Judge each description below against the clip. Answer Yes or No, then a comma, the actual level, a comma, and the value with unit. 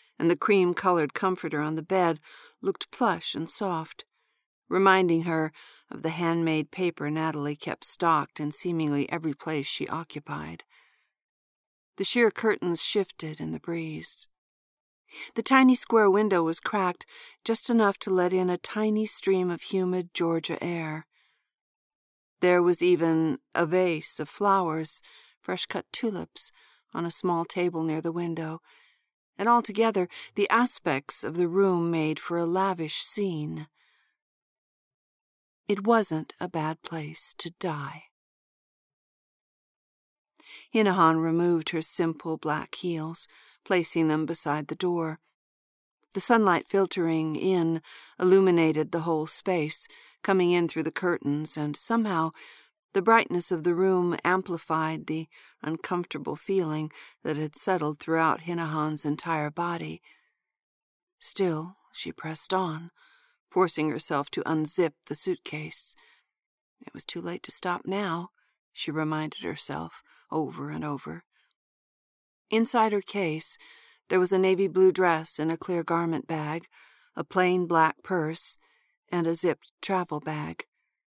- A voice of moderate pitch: Yes, medium, 170 Hz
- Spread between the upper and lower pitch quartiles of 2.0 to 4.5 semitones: Yes, average, 3.4 semitones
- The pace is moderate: No, slow, 130 wpm